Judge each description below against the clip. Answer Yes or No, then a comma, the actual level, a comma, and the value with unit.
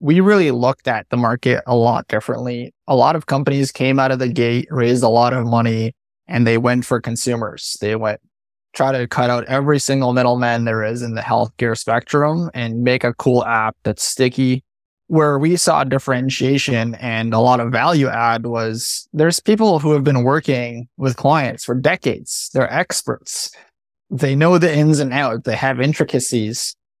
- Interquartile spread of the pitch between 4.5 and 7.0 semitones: No, average, 3.0 semitones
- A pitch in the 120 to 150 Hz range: Yes, low, 125 Hz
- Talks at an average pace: Yes, average, 180 wpm